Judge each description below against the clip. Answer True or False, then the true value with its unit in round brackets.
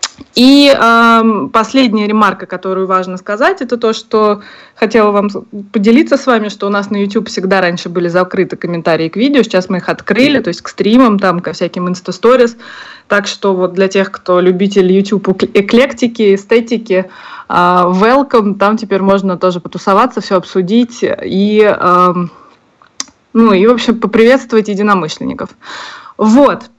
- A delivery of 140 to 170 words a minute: True (150 wpm)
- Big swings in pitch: False (3.7 semitones)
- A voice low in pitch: False (205 Hz)